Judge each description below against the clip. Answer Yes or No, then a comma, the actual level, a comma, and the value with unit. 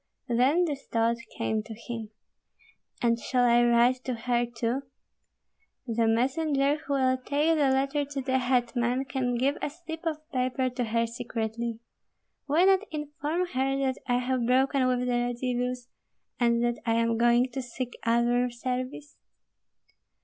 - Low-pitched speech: No, very high, 250 Hz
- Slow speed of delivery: No, average, 155 wpm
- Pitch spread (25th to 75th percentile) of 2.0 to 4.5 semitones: Yes, narrow, 2.4 semitones